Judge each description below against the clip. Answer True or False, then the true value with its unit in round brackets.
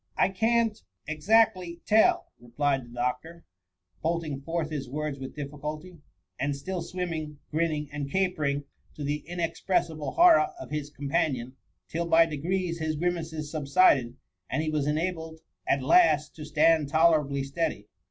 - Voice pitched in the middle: True (155 Hz)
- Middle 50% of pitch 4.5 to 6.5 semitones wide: False (3.0 semitones)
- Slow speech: False (150 wpm)